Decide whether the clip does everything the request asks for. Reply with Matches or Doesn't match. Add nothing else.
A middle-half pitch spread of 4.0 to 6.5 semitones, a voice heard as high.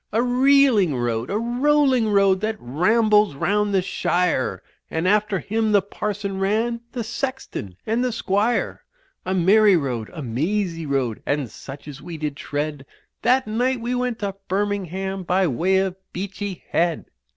Matches